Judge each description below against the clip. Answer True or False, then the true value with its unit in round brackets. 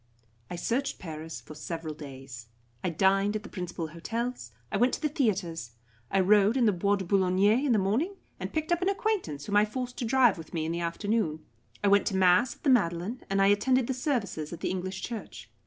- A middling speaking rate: False (220 wpm)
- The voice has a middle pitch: False (200 Hz)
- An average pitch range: False (6.2 semitones)